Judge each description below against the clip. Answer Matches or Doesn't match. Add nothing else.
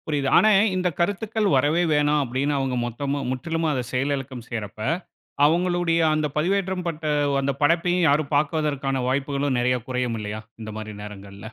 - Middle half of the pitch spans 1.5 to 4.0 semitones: Doesn't match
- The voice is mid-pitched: Matches